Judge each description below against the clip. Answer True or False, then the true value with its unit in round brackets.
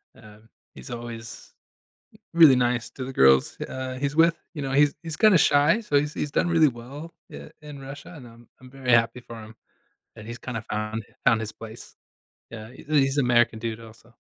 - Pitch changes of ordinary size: True (4.0 semitones)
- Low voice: True (125 Hz)